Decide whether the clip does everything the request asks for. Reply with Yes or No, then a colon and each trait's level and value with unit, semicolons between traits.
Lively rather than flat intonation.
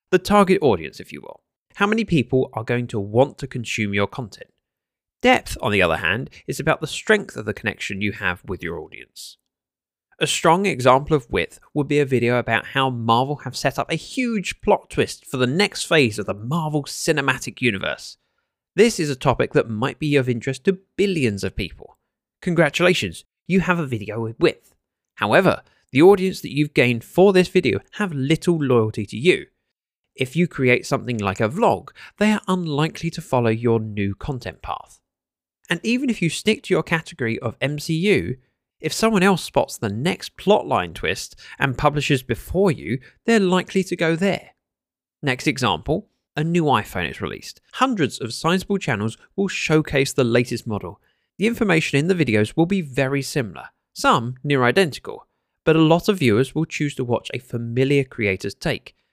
Yes: wide, 6.6 semitones